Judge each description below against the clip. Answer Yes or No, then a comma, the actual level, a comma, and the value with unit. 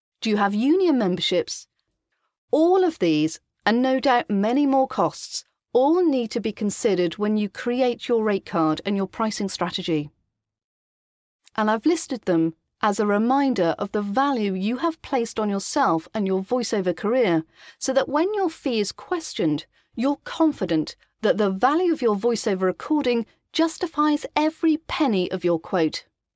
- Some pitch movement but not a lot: No, wide, 6.3 semitones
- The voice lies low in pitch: No, high, 220 Hz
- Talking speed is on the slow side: No, average, 155 wpm